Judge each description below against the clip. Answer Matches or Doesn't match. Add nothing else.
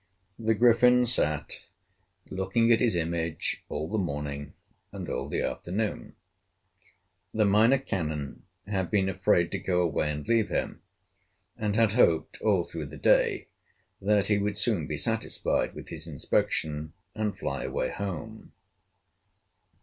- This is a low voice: Matches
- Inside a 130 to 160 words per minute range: Matches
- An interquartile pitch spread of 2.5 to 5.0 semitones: Doesn't match